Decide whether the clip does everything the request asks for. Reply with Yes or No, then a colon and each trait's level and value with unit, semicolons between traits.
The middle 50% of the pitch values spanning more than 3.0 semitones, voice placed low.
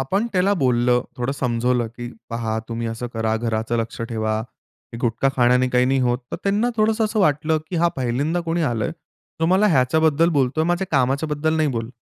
Yes: wide, 5.4 semitones; low, 130 Hz